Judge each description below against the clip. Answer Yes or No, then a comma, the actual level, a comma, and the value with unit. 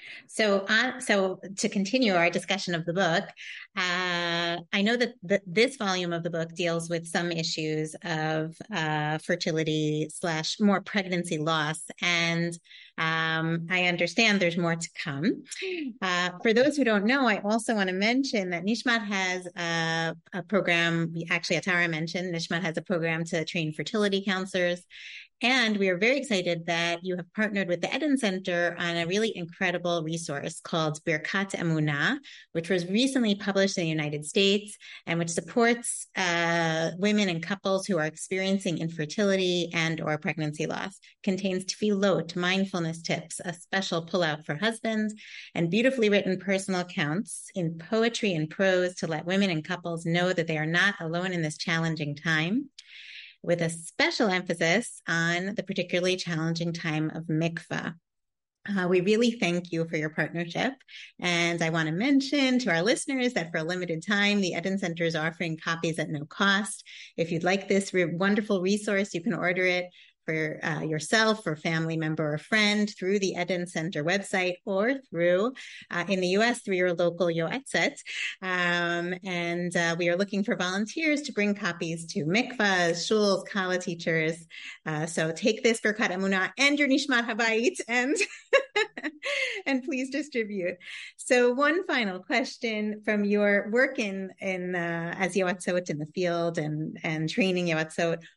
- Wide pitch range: No, average, 3.8 semitones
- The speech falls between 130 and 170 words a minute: Yes, average, 165 wpm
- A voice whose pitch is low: No, medium, 180 Hz